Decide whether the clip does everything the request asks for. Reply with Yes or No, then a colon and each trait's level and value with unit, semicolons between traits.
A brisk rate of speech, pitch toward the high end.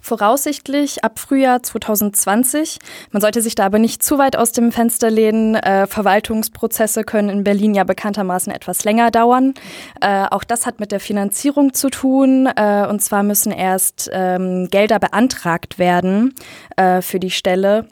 No: average, 160 wpm; high, 215 Hz